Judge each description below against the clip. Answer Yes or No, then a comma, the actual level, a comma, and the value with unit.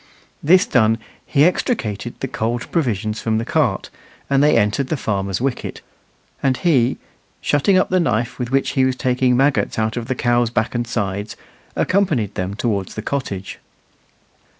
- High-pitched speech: No, low, 120 Hz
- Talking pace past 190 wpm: No, average, 165 wpm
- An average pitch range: Yes, average, 4.0 semitones